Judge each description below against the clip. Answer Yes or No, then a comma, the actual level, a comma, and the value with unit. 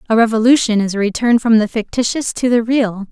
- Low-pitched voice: No, high, 225 Hz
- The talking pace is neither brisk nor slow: No, fast, 210 wpm